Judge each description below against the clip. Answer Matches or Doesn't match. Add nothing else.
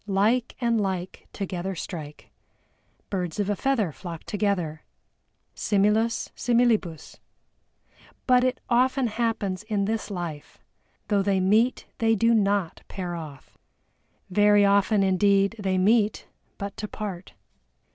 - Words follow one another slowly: Matches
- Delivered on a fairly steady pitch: Doesn't match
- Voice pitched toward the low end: Doesn't match